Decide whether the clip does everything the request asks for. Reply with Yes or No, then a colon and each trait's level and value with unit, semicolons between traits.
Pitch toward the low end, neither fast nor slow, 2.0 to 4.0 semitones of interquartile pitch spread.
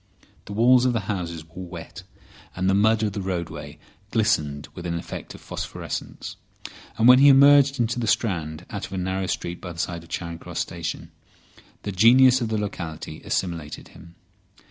No: very low, 95 Hz; average, 180 wpm; average, 5.0 semitones